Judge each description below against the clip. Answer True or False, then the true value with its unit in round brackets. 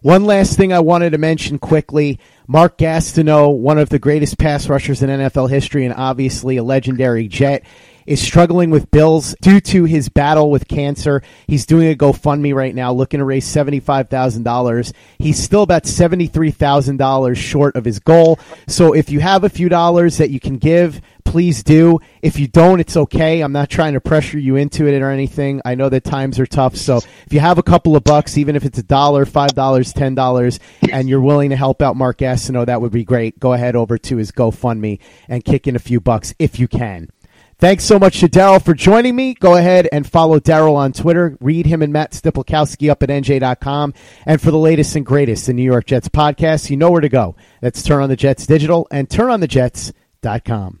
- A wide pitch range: False (3.5 semitones)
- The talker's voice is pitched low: False (145 Hz)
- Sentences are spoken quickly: True (210 wpm)